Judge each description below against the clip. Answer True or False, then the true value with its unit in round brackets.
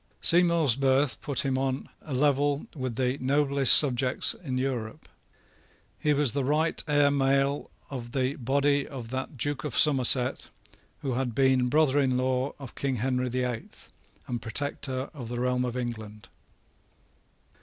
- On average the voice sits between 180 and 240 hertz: False (130 Hz)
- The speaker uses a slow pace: False (155 wpm)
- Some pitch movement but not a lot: False (2.0 semitones)